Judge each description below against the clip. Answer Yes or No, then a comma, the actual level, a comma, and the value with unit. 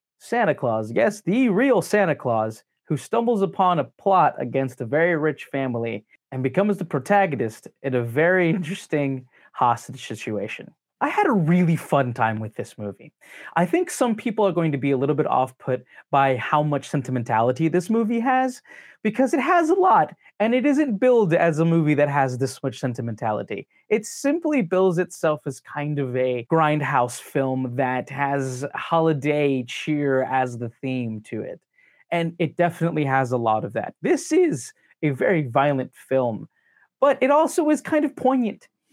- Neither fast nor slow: Yes, average, 175 wpm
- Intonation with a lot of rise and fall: Yes, wide, 7.7 semitones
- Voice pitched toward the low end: No, medium, 150 Hz